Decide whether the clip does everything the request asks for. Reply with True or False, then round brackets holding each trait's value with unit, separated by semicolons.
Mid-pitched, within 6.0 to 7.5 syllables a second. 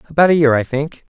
True (145 Hz; 6.8 syllables/s)